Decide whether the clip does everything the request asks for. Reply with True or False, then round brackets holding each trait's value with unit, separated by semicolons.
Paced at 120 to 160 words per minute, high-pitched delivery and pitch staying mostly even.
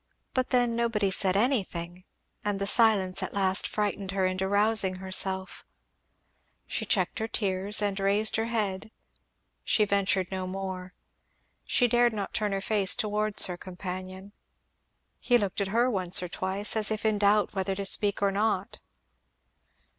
True (155 wpm; 200 Hz; 2.2 semitones)